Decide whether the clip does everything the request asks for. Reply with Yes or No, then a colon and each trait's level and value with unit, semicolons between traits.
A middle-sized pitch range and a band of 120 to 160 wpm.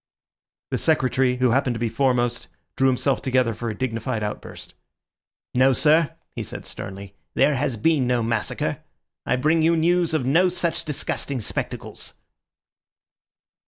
Yes: average, 4.3 semitones; average, 145 wpm